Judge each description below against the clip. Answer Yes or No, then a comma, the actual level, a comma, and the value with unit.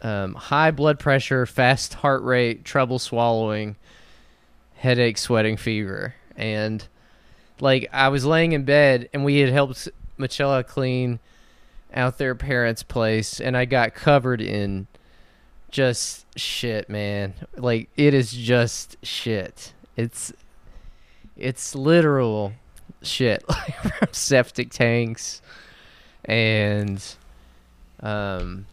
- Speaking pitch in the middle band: No, low, 120 Hz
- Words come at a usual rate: No, slow, 105 wpm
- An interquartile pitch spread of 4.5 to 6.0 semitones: No, average, 4.0 semitones